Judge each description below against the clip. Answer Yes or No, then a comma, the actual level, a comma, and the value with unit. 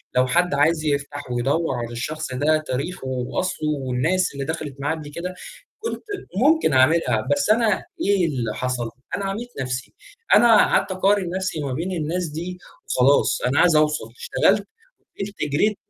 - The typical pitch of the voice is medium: Yes, medium, 155 Hz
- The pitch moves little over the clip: No, wide, 5.6 semitones